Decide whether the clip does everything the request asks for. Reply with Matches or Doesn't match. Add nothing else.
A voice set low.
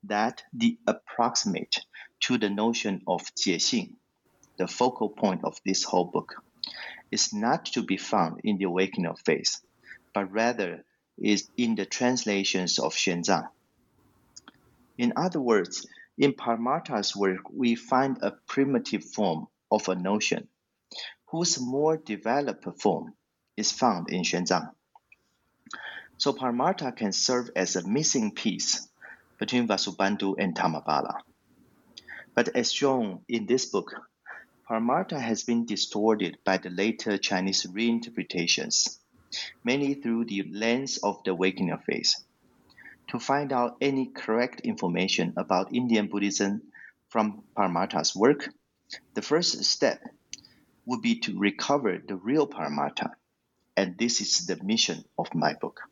Matches